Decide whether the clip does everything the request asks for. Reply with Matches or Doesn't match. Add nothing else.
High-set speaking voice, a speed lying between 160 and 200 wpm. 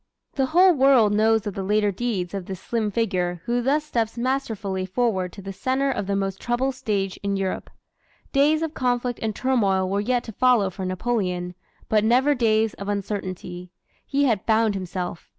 Matches